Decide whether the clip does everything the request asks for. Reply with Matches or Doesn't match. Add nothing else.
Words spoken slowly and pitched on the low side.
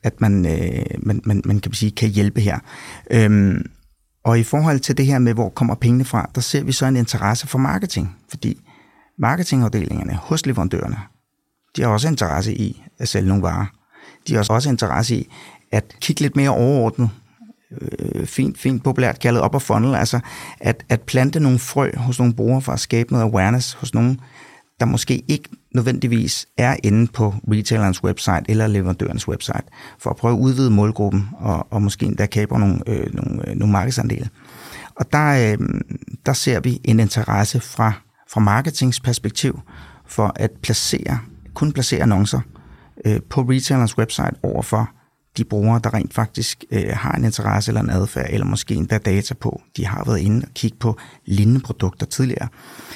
Doesn't match